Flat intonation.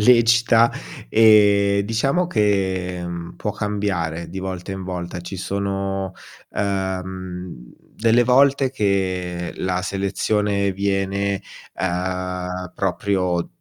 Yes: narrow, 2.2 semitones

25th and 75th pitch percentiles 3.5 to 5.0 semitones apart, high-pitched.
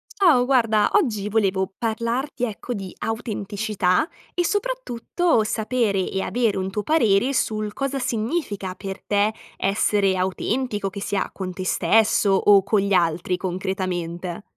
Yes: average, 3.8 semitones; high, 210 Hz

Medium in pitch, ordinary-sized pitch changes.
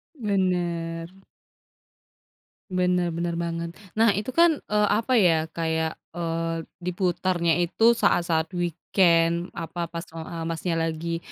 No: medium, 170 Hz; narrow, 1.7 semitones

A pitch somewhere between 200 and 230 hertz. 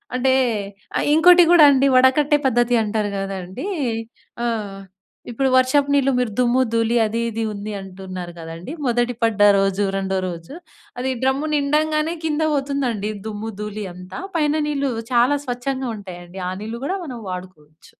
No: high, 240 Hz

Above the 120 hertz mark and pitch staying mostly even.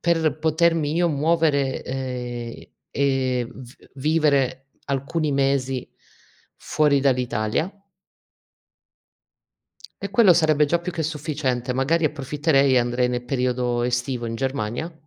No: medium, 140 Hz; average, 3.8 semitones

